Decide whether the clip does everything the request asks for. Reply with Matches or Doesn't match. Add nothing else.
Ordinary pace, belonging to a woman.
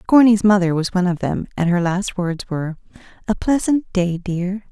Matches